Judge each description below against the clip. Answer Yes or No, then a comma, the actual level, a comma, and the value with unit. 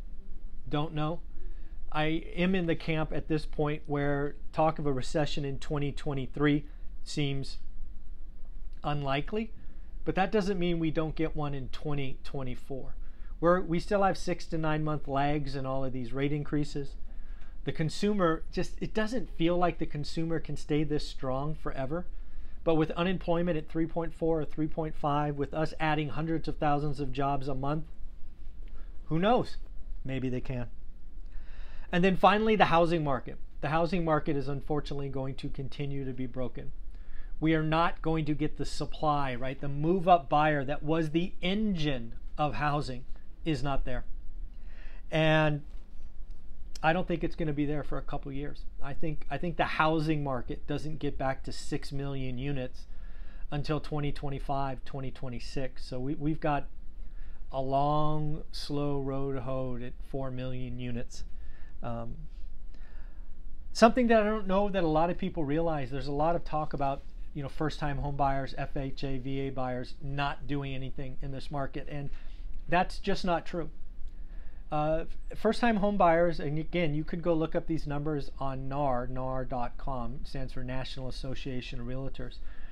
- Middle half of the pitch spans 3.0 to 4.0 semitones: Yes, average, 3.6 semitones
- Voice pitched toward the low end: No, medium, 145 Hz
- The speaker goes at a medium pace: Yes, average, 160 wpm